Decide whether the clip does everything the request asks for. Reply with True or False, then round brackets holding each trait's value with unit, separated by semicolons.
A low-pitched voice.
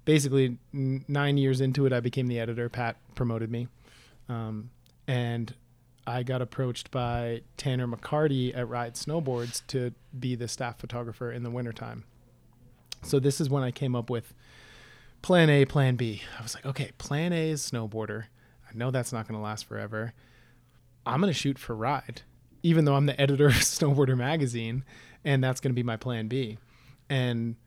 True (125 Hz)